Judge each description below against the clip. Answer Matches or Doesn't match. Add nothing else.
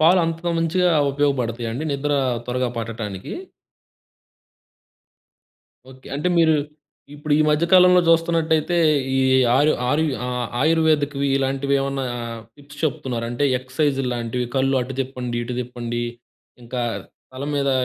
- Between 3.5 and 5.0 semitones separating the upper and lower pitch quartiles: Matches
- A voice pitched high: Doesn't match